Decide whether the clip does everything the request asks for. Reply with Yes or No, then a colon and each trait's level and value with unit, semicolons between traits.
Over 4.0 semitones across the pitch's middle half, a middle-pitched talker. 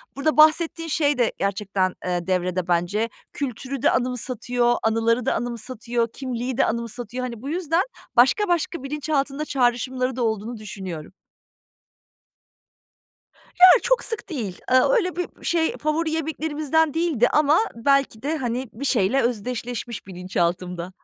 No: wide, 5.5 semitones; very high, 250 Hz